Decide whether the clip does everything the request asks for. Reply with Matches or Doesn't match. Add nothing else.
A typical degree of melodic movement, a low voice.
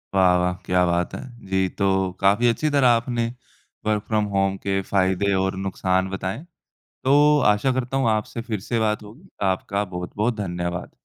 Matches